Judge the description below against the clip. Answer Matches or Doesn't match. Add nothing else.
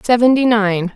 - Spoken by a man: Doesn't match